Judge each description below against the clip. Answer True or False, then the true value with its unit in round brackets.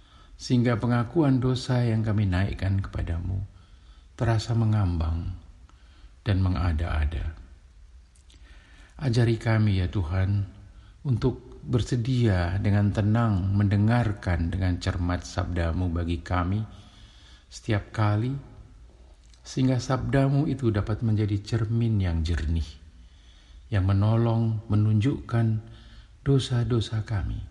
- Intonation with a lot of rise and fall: False (5.0 semitones)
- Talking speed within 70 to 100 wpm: True (85 wpm)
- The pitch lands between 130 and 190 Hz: False (100 Hz)